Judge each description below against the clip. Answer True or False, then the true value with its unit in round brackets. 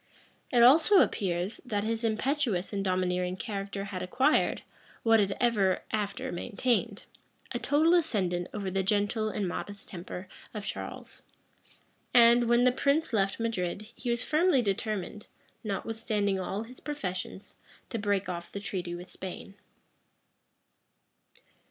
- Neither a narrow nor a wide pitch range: True (3.9 semitones)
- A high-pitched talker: True (210 Hz)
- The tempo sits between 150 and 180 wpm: False (135 wpm)